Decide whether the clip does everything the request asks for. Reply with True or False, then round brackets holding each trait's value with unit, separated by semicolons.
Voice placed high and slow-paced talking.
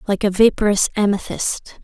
True (205 Hz; 130 wpm)